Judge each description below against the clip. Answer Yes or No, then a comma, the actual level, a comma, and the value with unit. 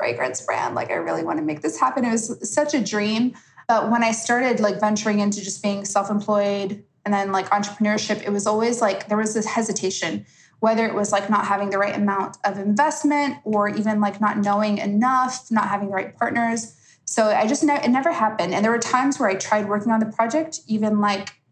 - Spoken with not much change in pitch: Yes, narrow, 2.3 semitones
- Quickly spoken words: Yes, fast, 225 wpm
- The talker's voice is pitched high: Yes, high, 210 Hz